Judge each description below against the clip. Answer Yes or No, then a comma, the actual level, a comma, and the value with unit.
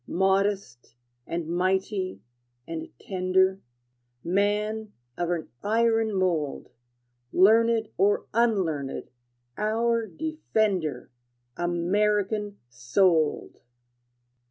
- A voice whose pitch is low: No, high, 195 Hz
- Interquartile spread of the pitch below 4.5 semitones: Yes, average, 3.7 semitones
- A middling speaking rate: No, slow, 70 wpm